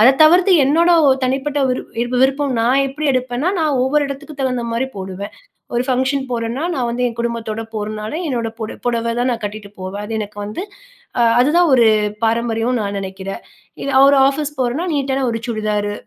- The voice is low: No, high, 245 Hz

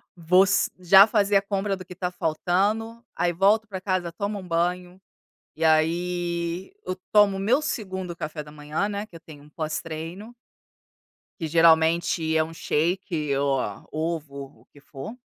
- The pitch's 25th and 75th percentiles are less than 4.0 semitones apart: Yes, average, 3.5 semitones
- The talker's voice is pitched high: No, medium, 175 Hz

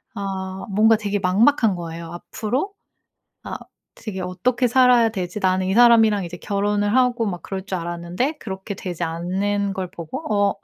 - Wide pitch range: No, average, 3.6 semitones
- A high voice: Yes, high, 200 Hz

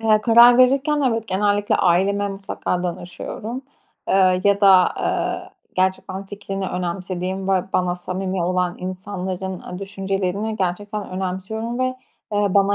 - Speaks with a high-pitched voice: Yes, high, 195 Hz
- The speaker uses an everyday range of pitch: No, narrow, 2.0 semitones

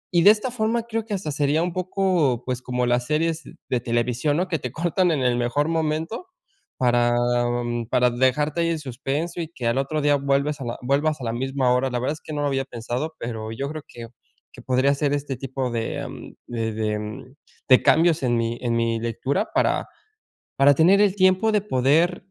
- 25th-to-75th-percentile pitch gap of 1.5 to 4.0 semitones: No, average, 5.0 semitones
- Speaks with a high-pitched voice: No, medium, 140 Hz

